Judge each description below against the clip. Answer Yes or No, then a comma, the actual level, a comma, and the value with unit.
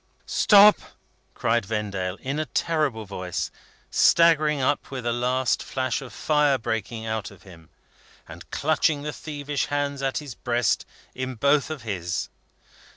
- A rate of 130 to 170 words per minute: Yes, average, 145 wpm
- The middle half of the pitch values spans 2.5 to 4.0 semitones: No, average, 4.9 semitones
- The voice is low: Yes, low, 130 Hz